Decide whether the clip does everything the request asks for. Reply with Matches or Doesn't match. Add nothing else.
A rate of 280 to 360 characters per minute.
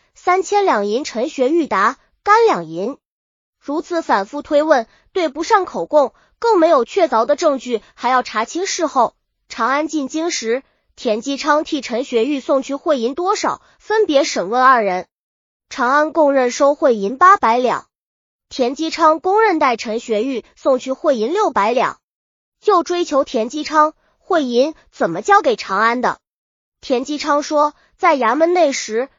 Doesn't match